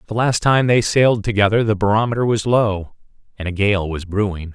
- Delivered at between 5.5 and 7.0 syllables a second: Yes, 5.6 syllables/s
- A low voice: Yes, low, 105 Hz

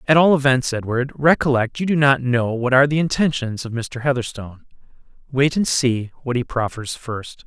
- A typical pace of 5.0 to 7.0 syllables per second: Yes, 5.2 syllables/s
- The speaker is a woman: No, male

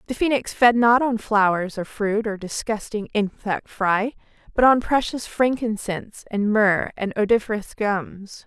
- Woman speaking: Yes, female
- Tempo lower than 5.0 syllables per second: Yes, 4.5 syllables/s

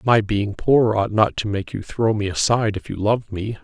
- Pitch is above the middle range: No, low, 105 Hz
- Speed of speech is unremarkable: No, fast, 250 wpm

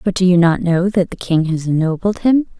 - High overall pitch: No, medium, 180 Hz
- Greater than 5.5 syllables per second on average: No, 5.4 syllables/s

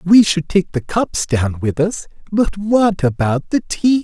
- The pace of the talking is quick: No, average, 195 wpm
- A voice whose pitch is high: No, medium, 180 Hz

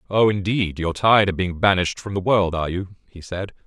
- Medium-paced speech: No, fast, 230 wpm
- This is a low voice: Yes, very low, 95 Hz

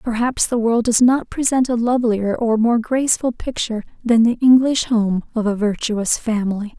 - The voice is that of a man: No, female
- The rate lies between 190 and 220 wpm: No, average, 175 wpm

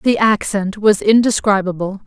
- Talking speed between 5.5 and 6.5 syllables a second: No, 4.5 syllables/s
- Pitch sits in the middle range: No, high, 210 Hz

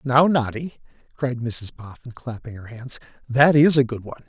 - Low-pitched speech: Yes, low, 125 Hz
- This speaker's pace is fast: No, average, 180 wpm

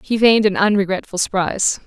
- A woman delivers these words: Yes, female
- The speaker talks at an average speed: Yes, average, 160 wpm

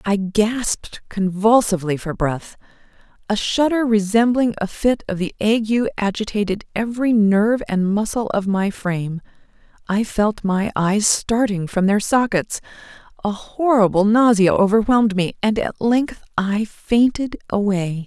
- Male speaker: No, female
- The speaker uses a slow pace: Yes, slow, 120 wpm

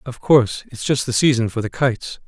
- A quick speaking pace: Yes, fast, 240 wpm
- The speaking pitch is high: No, low, 125 Hz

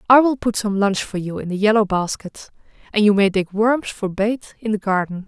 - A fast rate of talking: Yes, fast, 240 wpm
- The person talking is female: Yes, female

